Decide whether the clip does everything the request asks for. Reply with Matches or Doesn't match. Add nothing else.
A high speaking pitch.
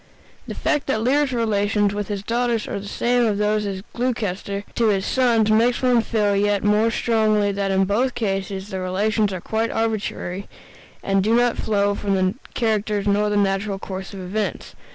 Matches